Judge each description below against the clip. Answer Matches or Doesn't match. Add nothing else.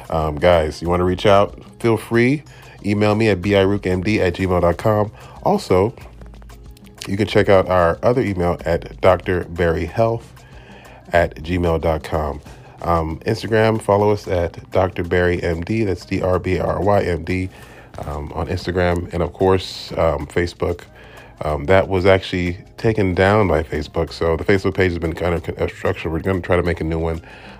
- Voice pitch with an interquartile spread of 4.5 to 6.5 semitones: Doesn't match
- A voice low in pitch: Matches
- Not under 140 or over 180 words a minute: Matches